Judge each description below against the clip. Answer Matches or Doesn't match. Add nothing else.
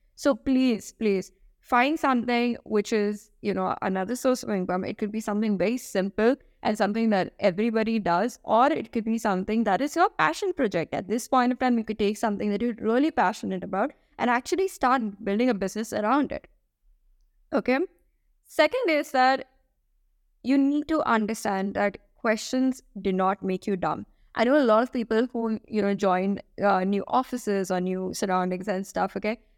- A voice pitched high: Matches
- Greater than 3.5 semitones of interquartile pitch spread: Matches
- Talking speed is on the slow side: Doesn't match